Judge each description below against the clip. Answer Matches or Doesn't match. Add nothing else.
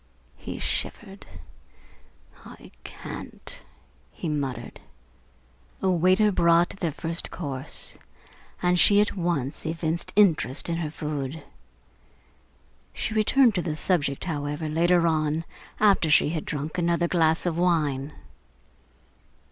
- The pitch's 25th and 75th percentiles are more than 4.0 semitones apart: Doesn't match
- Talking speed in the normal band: Doesn't match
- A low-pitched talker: Doesn't match